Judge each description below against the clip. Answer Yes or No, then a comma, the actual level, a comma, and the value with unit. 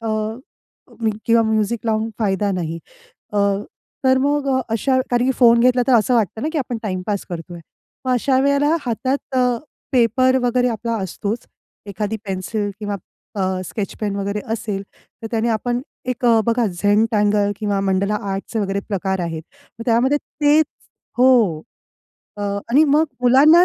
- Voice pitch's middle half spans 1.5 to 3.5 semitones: No, average, 3.9 semitones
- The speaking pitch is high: Yes, high, 225 Hz